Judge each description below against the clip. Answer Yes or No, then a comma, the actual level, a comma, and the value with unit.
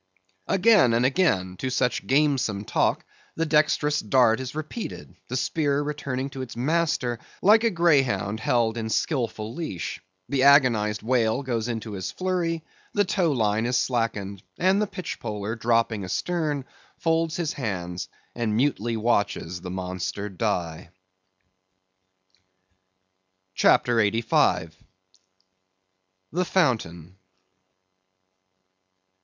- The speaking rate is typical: No, slow, 115 wpm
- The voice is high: No, low, 120 Hz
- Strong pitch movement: Yes, wide, 6.2 semitones